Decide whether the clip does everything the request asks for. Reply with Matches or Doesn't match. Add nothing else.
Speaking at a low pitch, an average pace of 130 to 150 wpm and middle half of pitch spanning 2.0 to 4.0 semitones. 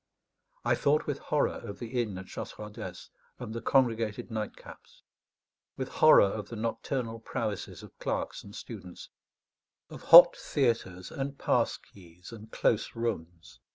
Matches